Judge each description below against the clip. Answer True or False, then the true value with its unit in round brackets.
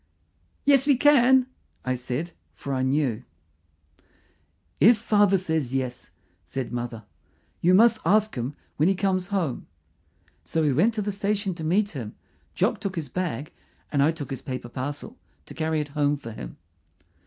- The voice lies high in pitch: False (160 Hz)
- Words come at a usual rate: True (165 wpm)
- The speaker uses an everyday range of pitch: False (7.2 semitones)